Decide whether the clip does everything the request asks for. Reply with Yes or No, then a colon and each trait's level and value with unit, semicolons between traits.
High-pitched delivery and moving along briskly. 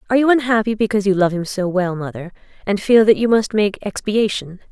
Yes: high, 205 Hz; fast, 215 wpm